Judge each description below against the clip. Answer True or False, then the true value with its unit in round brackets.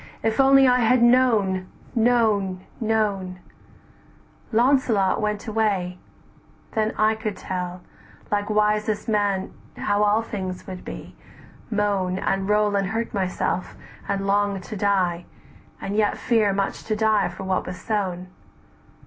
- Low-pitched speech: False (205 Hz)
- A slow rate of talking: True (130 wpm)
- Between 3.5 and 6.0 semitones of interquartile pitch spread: False (2.5 semitones)